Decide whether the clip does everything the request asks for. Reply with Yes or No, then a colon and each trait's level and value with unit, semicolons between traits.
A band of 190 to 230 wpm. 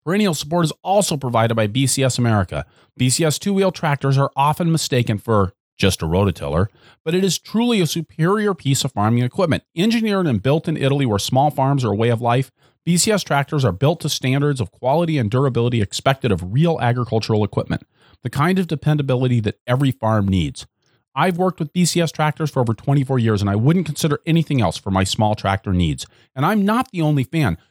Yes: average, 195 wpm